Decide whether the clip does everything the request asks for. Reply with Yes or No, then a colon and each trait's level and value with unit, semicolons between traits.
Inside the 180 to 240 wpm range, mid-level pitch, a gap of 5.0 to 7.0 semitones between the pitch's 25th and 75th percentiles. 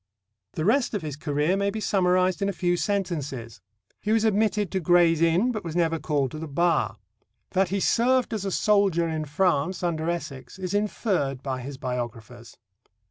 Yes: average, 185 wpm; medium, 175 Hz; average, 5.3 semitones